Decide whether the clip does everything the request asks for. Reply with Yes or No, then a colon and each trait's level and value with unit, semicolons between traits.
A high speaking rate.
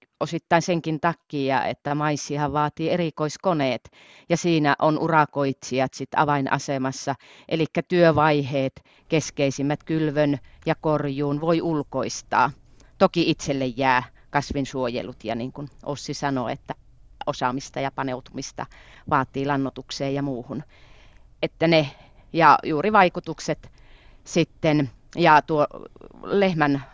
No: average, 105 wpm